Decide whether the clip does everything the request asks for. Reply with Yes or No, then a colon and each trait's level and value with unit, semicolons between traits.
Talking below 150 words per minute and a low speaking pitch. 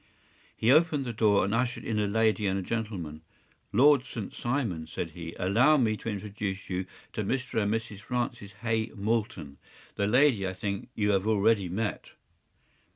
No: average, 170 wpm; low, 105 Hz